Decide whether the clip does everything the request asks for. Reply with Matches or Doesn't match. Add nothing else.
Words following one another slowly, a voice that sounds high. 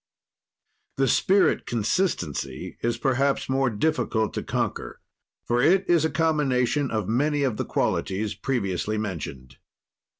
Doesn't match